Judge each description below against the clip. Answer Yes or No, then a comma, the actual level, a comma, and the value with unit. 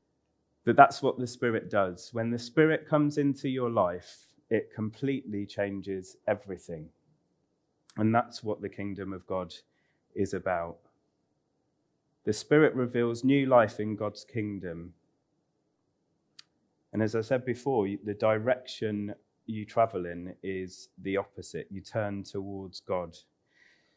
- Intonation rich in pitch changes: No, average, 3.7 semitones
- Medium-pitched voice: No, low, 105 Hz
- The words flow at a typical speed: No, slow, 130 wpm